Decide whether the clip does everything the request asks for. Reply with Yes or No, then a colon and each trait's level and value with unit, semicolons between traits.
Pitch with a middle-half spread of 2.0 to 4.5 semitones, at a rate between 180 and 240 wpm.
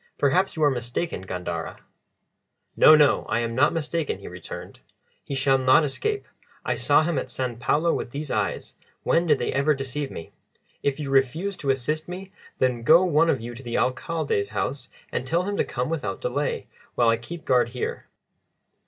Yes: average, 4.2 semitones; average, 190 wpm